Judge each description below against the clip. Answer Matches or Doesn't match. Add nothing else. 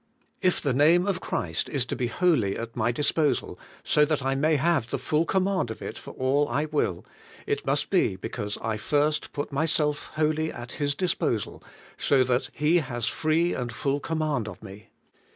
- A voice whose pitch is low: Doesn't match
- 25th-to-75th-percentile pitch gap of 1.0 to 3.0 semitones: Doesn't match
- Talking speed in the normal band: Matches